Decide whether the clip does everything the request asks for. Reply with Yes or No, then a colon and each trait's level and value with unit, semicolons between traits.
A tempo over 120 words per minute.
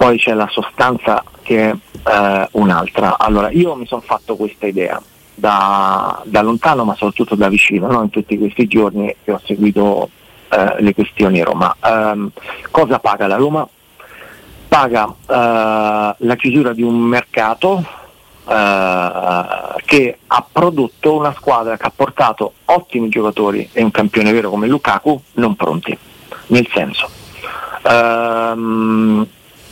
Yes: average, 140 wpm